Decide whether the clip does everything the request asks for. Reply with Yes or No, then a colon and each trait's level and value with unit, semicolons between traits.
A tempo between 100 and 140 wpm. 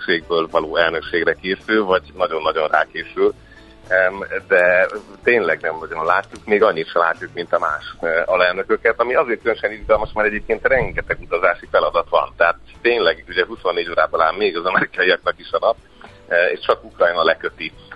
No: fast, 155 wpm